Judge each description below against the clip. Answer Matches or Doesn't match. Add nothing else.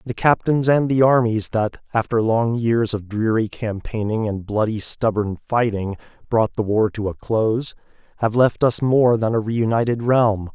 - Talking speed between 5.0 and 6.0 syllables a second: Doesn't match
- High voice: Doesn't match